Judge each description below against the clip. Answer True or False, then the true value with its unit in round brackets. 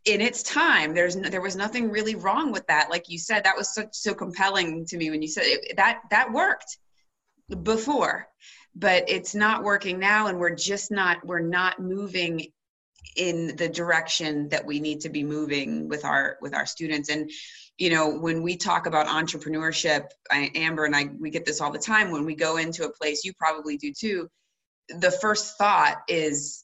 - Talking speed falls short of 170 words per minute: False (200 wpm)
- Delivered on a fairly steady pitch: False (4.4 semitones)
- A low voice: False (170 Hz)